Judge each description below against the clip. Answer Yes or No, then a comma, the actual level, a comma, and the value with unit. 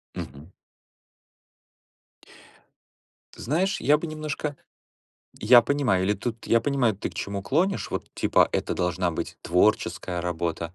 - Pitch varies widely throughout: Yes, wide, 8.3 semitones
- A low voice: Yes, low, 105 Hz